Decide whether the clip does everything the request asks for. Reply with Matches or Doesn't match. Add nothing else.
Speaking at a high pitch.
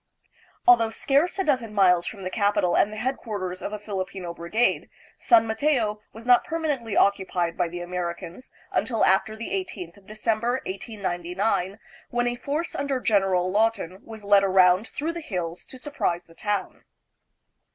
Matches